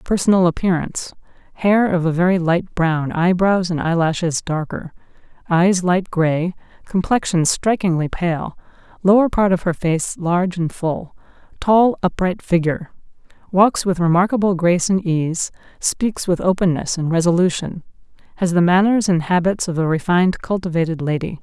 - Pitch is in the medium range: Yes, medium, 180 Hz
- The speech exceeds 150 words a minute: No, slow, 135 wpm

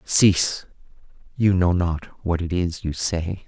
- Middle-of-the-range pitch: No, very low, 90 Hz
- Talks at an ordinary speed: Yes, average, 155 wpm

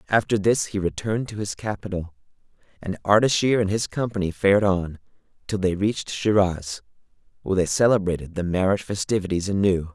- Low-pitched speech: Yes, low, 100 Hz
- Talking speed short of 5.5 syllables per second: No, 5.9 syllables/s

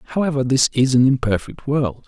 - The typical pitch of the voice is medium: No, low, 130 Hz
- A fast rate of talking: No, average, 175 wpm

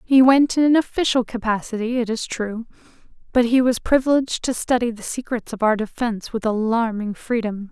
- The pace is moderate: Yes, average, 180 wpm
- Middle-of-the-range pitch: No, high, 235 Hz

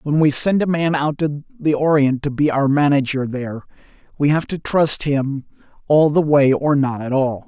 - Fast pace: Yes, fast, 210 wpm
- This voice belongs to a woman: No, male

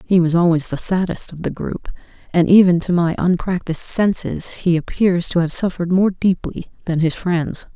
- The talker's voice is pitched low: No, medium, 175 Hz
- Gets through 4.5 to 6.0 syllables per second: Yes, 5.1 syllables/s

